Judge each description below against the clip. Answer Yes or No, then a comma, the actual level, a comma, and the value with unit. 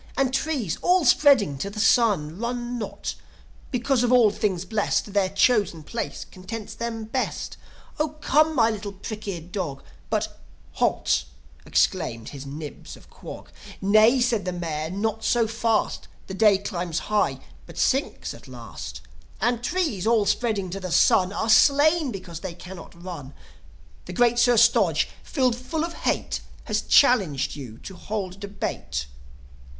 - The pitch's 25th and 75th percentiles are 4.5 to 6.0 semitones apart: Yes, average, 5.0 semitones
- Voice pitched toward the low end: No, high, 210 Hz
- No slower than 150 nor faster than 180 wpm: Yes, average, 155 wpm